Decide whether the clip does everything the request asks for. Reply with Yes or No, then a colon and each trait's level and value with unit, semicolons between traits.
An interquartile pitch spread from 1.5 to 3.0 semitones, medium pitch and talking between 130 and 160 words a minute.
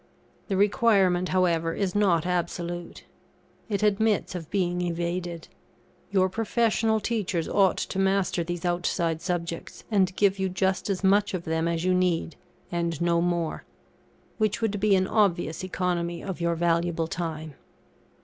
Yes: narrow, 2.5 semitones; medium, 180 Hz; average, 145 wpm